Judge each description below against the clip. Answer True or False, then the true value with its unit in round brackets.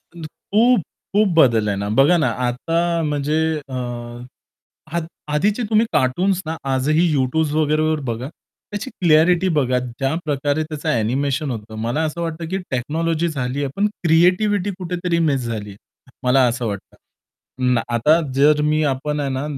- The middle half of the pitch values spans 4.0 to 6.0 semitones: True (4.6 semitones)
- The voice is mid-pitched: True (150 Hz)